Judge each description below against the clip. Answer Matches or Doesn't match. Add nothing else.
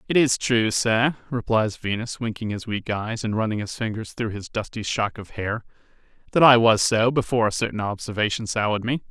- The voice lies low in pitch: Matches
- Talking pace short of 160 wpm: Doesn't match